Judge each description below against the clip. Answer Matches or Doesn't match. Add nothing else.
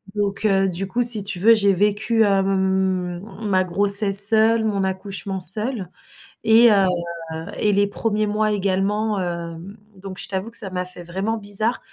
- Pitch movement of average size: Doesn't match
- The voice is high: Matches